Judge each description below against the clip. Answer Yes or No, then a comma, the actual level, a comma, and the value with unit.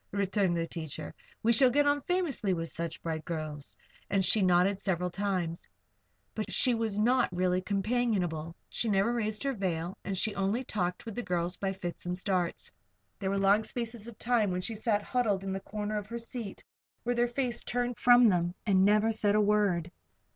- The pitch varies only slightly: No, average, 4.3 semitones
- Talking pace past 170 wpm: Yes, average, 195 wpm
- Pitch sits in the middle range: No, high, 200 Hz